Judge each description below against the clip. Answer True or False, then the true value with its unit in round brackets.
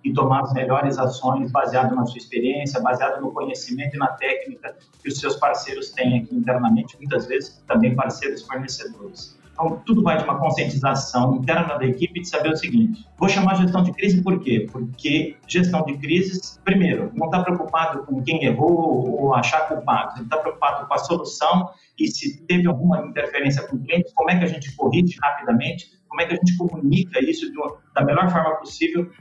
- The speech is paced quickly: True (195 wpm)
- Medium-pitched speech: True (160 Hz)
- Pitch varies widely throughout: False (5.0 semitones)